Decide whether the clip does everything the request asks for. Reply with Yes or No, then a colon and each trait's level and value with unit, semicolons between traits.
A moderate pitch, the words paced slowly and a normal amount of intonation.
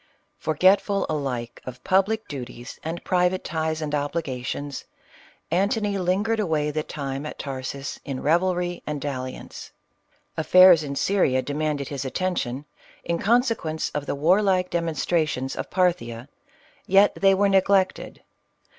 Yes: medium, 160 Hz; slow, 130 wpm; average, 5.0 semitones